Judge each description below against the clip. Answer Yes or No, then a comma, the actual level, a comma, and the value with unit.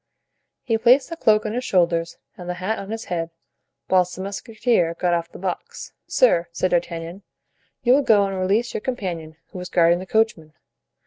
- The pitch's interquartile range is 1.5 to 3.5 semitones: No, average, 4.4 semitones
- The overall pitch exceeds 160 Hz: Yes, medium, 185 Hz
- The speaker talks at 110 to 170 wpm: No, average, 190 wpm